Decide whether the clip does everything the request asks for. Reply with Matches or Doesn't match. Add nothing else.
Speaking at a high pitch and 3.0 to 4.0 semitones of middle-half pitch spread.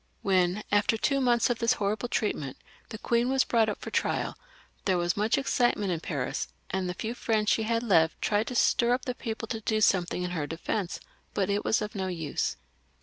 Doesn't match